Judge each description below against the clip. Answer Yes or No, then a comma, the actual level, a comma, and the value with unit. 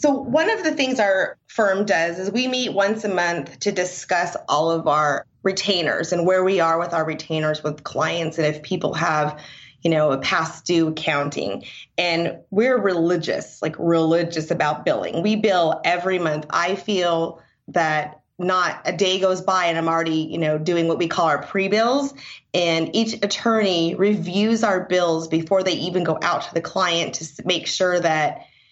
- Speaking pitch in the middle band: Yes, medium, 175 Hz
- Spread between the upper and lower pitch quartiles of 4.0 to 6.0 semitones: No, average, 3.2 semitones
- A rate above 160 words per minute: Yes, average, 185 wpm